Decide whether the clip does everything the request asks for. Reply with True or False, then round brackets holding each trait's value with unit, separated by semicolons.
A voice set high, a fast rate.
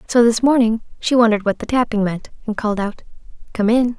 True (225 Hz; 210 wpm)